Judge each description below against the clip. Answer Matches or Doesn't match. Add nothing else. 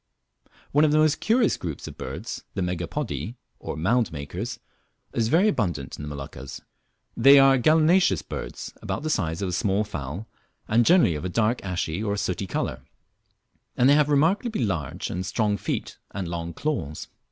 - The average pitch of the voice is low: Matches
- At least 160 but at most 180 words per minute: Matches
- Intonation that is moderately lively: Doesn't match